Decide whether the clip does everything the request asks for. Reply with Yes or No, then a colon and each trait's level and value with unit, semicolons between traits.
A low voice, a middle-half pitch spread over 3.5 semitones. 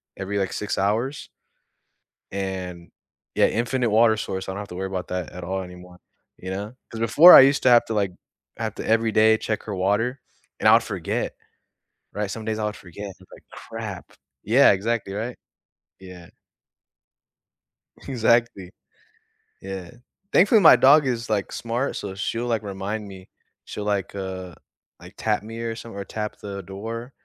No: low, 105 Hz; average, 3.2 semitones